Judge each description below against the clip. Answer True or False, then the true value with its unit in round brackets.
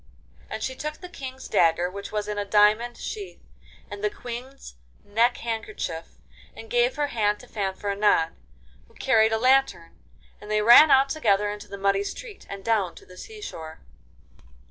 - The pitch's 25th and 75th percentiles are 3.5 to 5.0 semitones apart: True (4.6 semitones)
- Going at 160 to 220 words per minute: True (170 wpm)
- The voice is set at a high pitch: True (220 Hz)